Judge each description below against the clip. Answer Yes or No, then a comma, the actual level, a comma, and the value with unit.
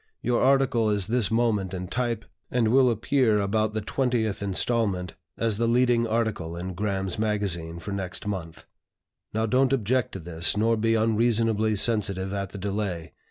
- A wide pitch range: No, average, 3.1 semitones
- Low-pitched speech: Yes, low, 110 Hz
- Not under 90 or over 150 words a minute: No, average, 160 wpm